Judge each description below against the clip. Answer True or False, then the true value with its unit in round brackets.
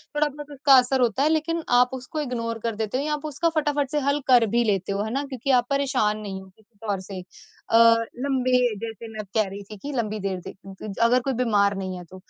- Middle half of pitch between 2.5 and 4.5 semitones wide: False (5.2 semitones)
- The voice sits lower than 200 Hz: False (235 Hz)